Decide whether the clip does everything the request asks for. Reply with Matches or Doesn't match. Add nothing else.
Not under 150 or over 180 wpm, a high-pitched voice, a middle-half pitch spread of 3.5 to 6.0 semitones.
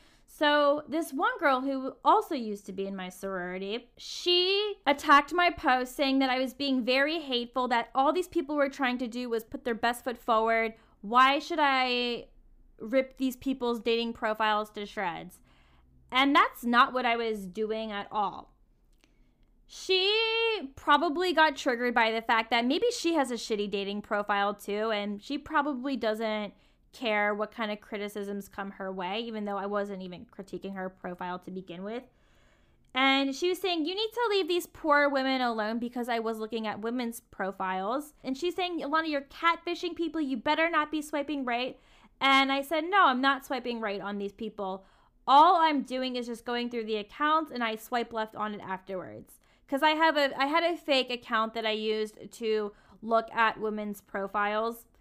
Doesn't match